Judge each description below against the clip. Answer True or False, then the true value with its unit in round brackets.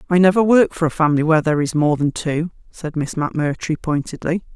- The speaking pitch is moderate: True (160 Hz)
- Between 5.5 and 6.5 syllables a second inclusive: True (6.3 syllables/s)